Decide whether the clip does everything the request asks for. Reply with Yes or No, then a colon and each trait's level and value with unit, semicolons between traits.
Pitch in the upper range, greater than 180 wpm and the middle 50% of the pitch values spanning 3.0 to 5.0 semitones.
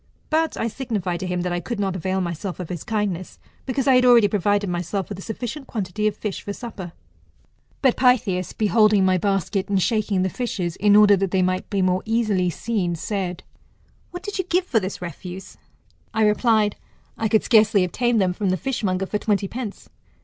Yes: high, 205 Hz; average, 200 wpm; average, 3.5 semitones